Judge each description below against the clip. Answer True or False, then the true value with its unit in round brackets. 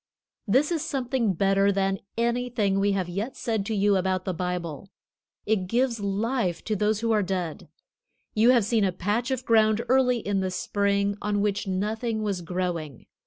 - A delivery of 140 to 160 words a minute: False (175 wpm)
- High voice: True (205 Hz)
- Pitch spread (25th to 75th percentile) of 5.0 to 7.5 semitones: False (3.3 semitones)